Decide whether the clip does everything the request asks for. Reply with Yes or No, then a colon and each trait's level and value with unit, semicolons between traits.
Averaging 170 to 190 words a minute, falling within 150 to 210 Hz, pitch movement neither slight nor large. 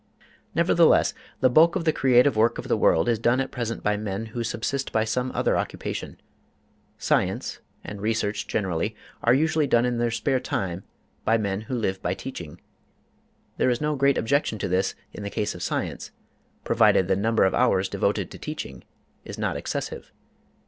No: average, 180 wpm; low, 115 Hz; average, 4.1 semitones